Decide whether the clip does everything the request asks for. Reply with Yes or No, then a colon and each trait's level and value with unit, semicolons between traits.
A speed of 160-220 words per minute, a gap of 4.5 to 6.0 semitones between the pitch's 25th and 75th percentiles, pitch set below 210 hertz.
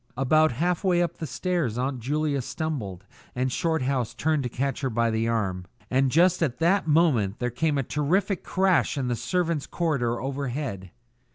Yes: average, 175 wpm; average, 4.9 semitones; medium, 140 Hz